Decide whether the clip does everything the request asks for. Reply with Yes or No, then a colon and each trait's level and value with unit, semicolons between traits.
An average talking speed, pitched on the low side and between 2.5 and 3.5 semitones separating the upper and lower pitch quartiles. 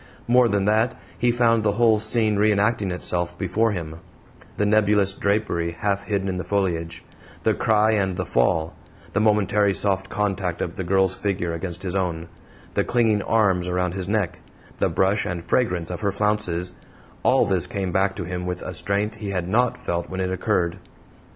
Yes: average, 185 wpm; very low, 95 Hz; average, 2.9 semitones